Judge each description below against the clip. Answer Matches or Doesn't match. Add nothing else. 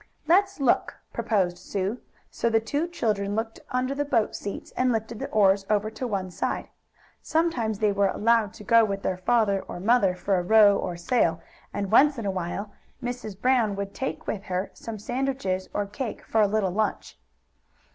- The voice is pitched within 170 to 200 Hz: Doesn't match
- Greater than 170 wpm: Matches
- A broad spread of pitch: Doesn't match